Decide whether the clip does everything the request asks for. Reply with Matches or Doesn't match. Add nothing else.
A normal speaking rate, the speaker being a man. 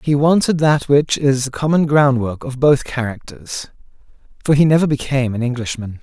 Matches